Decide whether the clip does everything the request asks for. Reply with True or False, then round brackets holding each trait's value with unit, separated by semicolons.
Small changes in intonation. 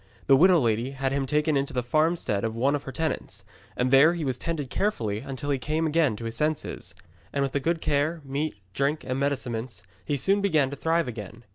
False (3.6 semitones)